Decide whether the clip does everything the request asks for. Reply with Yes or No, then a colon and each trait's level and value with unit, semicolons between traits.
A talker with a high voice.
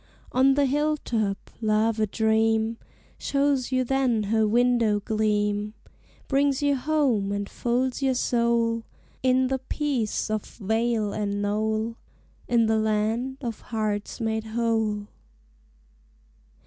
Yes: high, 225 Hz